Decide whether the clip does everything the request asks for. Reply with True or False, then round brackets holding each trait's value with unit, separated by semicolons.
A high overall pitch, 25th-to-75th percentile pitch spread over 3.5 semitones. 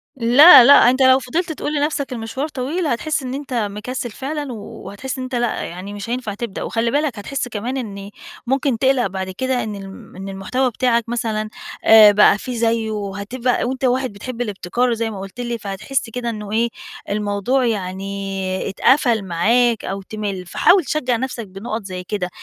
True (230 Hz; 4.2 semitones)